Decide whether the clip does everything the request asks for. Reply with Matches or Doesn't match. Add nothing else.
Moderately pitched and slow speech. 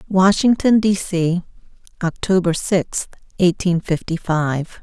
Matches